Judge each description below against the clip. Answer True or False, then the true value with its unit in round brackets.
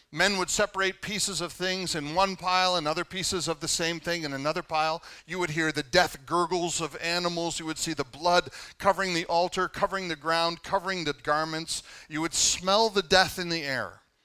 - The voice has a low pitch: False (170 Hz)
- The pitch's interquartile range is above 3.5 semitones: False (2.7 semitones)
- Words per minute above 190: True (205 wpm)